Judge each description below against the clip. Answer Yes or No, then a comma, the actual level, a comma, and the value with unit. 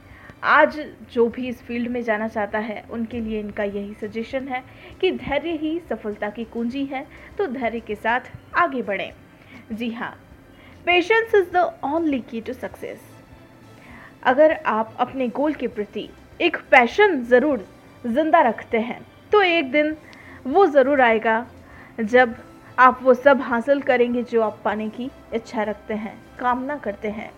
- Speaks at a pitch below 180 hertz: No, high, 245 Hz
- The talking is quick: No, average, 155 wpm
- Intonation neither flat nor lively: Yes, average, 4.6 semitones